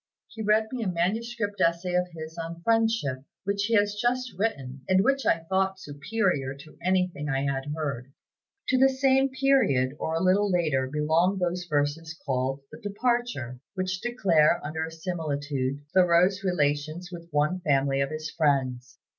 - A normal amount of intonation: No, wide, 5.8 semitones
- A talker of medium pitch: Yes, medium, 170 Hz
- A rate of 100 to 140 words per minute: No, average, 165 wpm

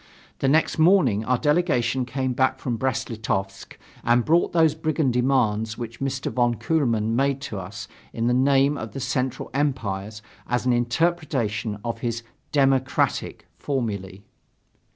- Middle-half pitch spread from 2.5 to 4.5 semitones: Yes, average, 3.3 semitones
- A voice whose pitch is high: No, low, 125 Hz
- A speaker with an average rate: Yes, average, 145 wpm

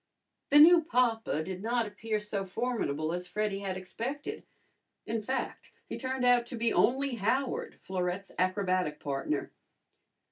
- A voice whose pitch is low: No, high, 215 Hz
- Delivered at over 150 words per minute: No, average, 140 wpm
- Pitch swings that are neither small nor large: Yes, average, 5.0 semitones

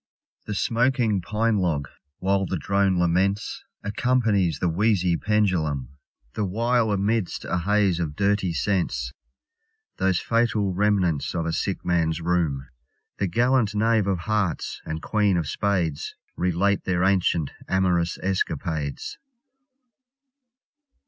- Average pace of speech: No, slow, 120 wpm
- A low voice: Yes, very low, 95 Hz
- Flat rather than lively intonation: No, average, 3.5 semitones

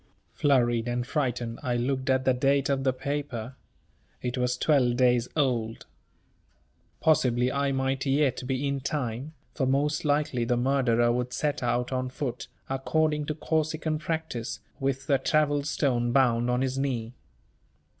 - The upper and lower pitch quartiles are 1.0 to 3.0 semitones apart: Yes, narrow, 2.6 semitones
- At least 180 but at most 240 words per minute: No, average, 150 wpm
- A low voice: Yes, low, 130 Hz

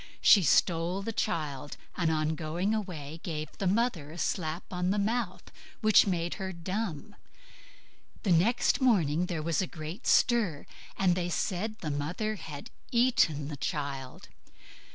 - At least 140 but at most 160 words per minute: Yes, average, 145 wpm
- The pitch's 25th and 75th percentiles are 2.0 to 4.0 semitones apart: No, average, 4.7 semitones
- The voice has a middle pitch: Yes, medium, 175 Hz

